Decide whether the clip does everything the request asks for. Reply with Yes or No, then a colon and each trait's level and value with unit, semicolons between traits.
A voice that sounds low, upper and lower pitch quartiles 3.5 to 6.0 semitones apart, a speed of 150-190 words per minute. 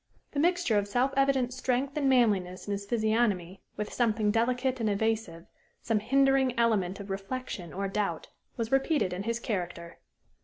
No: high, 225 Hz; average, 4.4 semitones; average, 160 wpm